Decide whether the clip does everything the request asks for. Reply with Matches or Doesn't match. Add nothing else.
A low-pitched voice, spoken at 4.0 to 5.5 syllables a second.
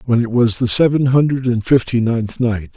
Matches